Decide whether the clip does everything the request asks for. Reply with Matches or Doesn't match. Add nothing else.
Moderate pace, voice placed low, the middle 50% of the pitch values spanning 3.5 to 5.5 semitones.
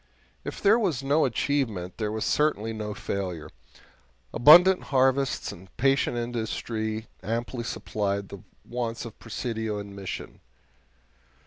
Doesn't match